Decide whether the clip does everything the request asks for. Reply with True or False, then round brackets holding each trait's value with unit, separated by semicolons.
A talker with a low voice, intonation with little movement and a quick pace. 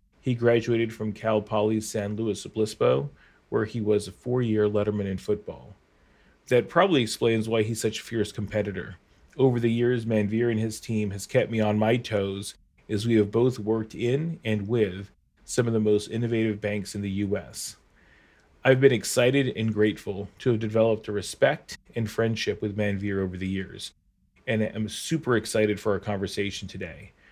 False (110 Hz; 1.9 semitones; 175 wpm)